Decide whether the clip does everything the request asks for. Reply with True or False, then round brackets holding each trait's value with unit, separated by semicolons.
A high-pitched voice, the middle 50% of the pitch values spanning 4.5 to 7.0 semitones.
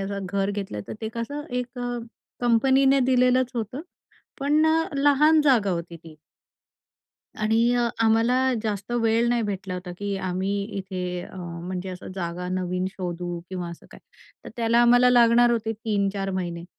True (210 Hz; 4.8 semitones)